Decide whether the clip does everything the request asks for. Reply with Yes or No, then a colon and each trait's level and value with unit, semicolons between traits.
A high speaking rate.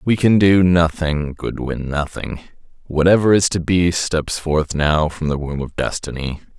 No: average, 155 wpm